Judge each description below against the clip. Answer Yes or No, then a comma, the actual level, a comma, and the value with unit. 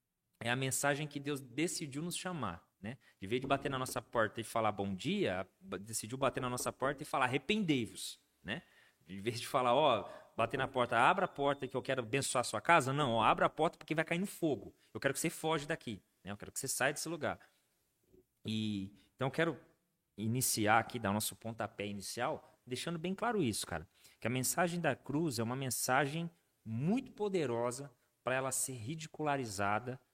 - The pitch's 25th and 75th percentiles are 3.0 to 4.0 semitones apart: No, wide, 5.6 semitones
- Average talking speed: No, fast, 200 wpm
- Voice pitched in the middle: No, low, 130 Hz